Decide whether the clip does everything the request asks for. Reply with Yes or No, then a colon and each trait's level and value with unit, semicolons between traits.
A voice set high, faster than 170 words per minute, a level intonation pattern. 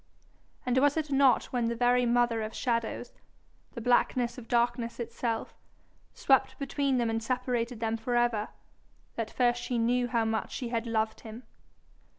No: high, 240 Hz; average, 160 wpm; narrow, 1.5 semitones